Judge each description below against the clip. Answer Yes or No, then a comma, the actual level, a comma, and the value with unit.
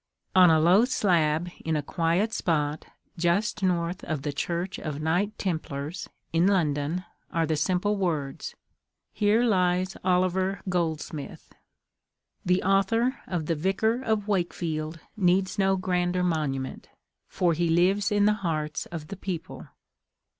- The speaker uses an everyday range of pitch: Yes, average, 3.3 semitones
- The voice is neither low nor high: Yes, medium, 180 Hz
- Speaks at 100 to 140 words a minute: Yes, slow, 135 wpm